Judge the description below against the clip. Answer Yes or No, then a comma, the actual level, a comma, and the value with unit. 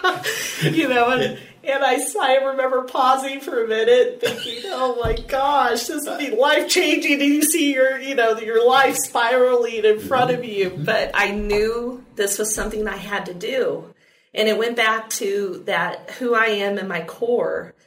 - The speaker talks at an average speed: Yes, average, 185 wpm